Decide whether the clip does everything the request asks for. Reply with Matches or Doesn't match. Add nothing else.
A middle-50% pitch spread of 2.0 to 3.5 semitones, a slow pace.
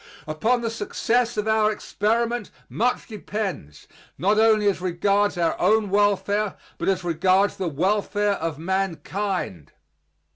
Matches